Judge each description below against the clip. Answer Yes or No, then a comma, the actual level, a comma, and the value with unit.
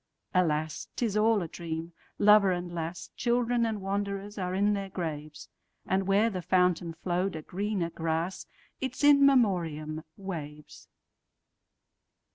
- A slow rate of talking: Yes, slow, 115 wpm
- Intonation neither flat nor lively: Yes, average, 4.0 semitones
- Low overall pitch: No, medium, 185 Hz